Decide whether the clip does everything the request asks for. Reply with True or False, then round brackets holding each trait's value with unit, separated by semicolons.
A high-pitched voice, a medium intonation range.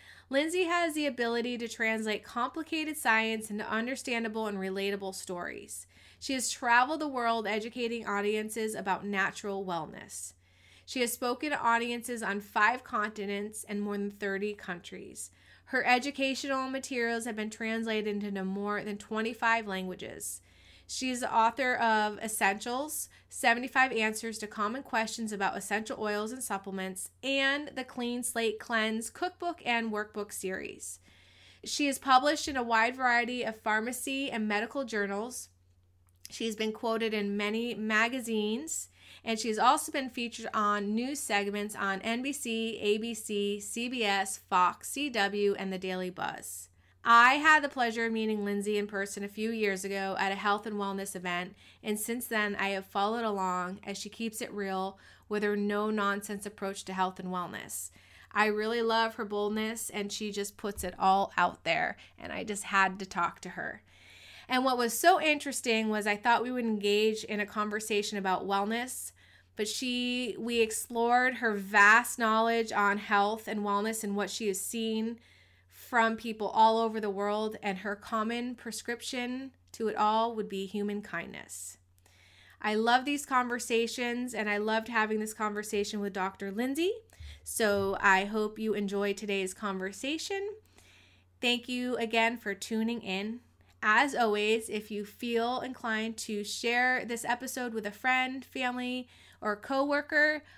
True (215 Hz; 3.0 semitones)